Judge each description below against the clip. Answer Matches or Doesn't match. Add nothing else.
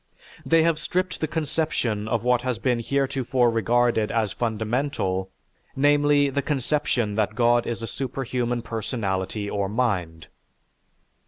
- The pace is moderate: Doesn't match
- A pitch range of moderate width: Matches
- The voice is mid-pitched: Doesn't match